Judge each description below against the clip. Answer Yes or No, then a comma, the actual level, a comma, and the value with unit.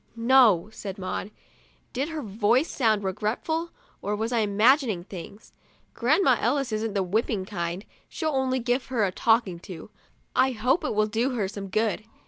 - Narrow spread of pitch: No, average, 4.3 semitones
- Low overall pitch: No, high, 220 Hz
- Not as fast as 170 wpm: No, average, 180 wpm